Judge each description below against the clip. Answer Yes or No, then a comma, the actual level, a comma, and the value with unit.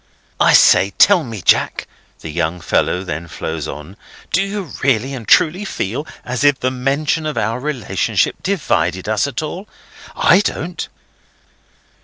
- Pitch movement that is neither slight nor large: No, wide, 8.7 semitones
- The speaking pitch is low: Yes, low, 130 Hz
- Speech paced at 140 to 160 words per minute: Yes, average, 150 wpm